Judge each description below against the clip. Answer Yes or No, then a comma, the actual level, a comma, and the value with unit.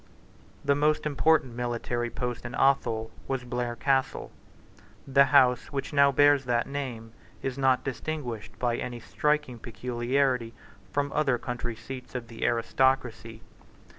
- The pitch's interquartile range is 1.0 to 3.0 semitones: Yes, narrow, 2.6 semitones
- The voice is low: Yes, low, 125 Hz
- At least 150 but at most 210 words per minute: No, slow, 135 wpm